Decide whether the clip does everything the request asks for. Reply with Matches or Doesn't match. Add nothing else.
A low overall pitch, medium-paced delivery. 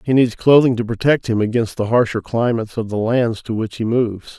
Doesn't match